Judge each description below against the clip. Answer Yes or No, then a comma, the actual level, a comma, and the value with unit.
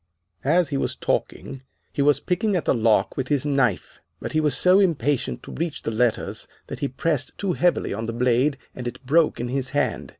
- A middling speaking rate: No, fast, 210 wpm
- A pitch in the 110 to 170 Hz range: Yes, medium, 140 Hz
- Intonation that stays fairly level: No, average, 4.3 semitones